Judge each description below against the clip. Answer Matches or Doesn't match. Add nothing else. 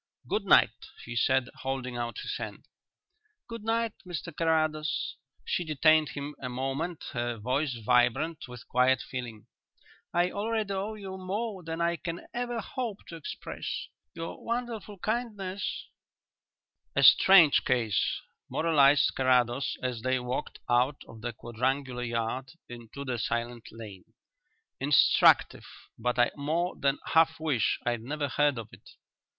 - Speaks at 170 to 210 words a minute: Doesn't match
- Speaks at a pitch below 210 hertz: Matches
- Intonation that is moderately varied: Doesn't match